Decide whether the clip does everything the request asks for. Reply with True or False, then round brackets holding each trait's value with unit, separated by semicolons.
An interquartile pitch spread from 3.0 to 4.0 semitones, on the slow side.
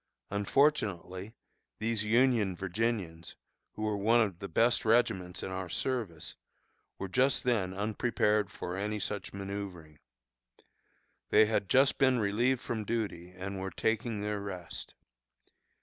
True (3.5 semitones; 130 wpm)